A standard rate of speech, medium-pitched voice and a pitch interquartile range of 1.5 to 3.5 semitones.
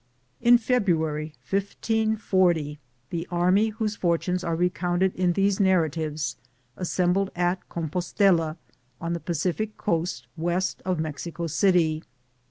No: slow, 120 wpm; medium, 175 Hz; average, 3.0 semitones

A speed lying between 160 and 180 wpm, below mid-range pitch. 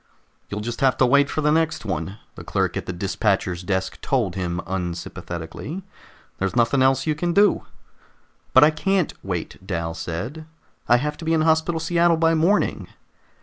Yes: average, 175 wpm; low, 130 Hz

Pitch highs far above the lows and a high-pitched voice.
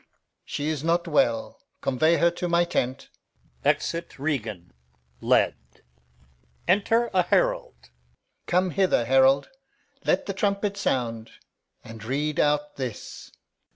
No: wide, 5.8 semitones; medium, 150 Hz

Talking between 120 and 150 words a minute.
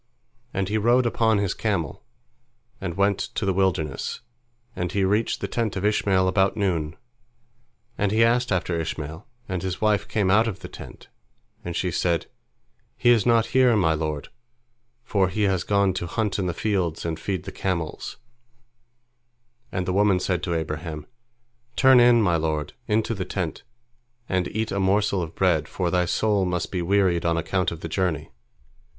No: average, 175 wpm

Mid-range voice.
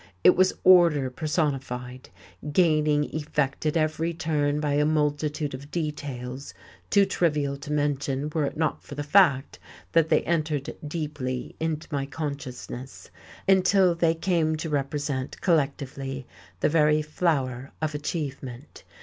Yes: medium, 150 Hz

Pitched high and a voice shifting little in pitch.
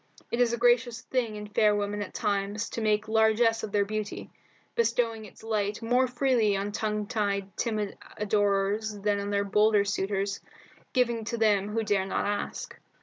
Yes: high, 210 Hz; narrow, 1.9 semitones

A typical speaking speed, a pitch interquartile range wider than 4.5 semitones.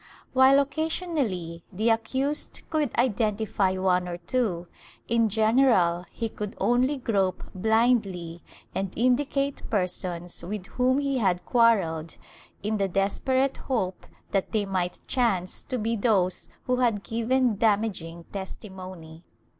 No: slow, 120 wpm; average, 5.3 semitones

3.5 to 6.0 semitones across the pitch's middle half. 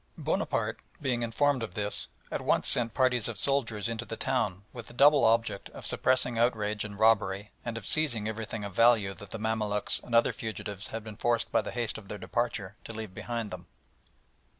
No: narrow, 2.4 semitones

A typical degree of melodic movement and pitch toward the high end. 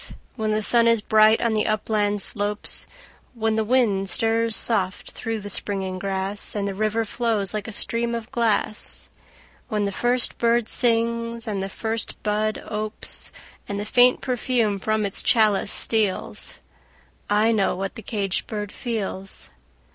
No: narrow, 2.0 semitones; high, 215 Hz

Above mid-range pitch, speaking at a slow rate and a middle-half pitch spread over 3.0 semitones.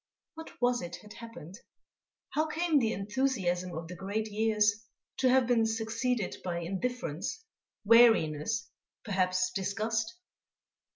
Yes: high, 220 Hz; slow, 120 wpm; average, 4.7 semitones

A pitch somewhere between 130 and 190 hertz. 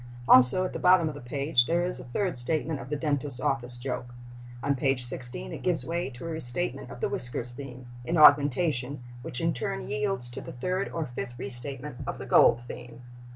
Yes: low, 135 Hz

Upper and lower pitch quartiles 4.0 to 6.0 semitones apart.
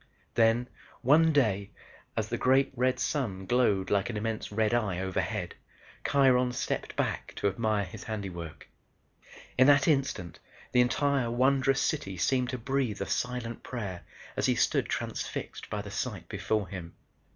Yes: average, 4.5 semitones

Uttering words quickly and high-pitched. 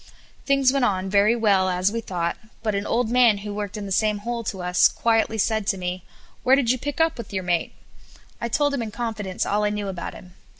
Yes: fast, 240 wpm; high, 210 Hz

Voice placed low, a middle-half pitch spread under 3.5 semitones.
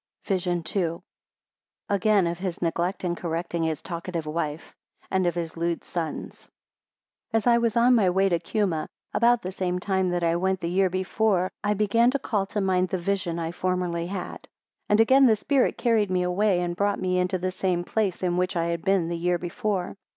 No: medium, 185 Hz; average, 2.7 semitones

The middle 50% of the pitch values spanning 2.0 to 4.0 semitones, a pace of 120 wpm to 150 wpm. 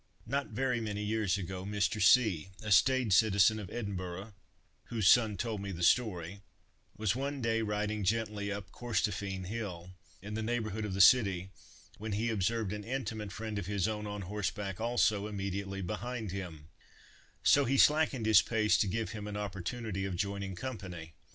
No: narrow, 2.6 semitones; average, 165 wpm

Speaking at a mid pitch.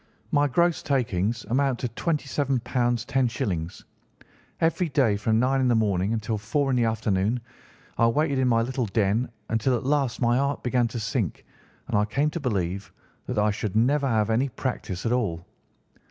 No: low, 120 Hz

